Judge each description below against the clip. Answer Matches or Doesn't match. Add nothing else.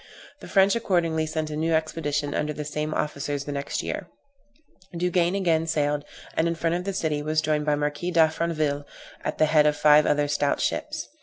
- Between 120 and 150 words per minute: Doesn't match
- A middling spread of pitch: Doesn't match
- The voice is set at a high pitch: Doesn't match